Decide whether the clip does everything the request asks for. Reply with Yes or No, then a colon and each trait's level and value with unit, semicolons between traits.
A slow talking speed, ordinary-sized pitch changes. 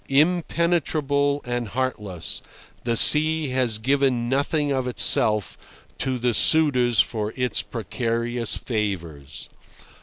Yes: slow, 100 wpm; average, 3.8 semitones